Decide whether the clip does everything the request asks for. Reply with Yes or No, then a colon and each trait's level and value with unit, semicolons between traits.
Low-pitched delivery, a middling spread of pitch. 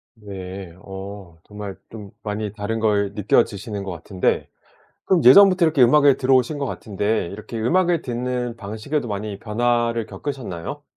Yes: low, 110 Hz; average, 4.1 semitones